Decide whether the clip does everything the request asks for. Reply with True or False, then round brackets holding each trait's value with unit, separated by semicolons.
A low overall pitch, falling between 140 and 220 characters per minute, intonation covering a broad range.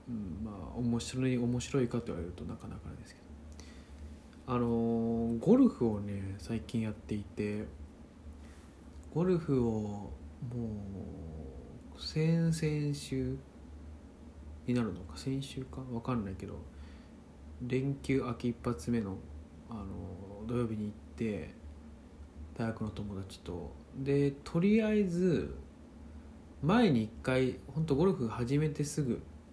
True (105 Hz; 215 characters per minute; 8.7 semitones)